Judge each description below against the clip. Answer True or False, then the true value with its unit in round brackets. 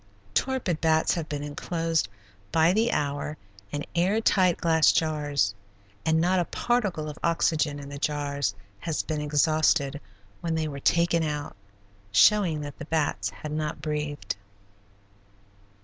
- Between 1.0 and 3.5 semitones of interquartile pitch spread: True (2.4 semitones)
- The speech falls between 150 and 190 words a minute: False (140 wpm)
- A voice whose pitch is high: False (155 Hz)